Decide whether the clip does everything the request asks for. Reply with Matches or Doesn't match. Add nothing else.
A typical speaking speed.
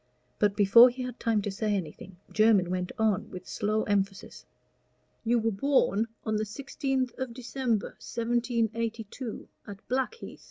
Matches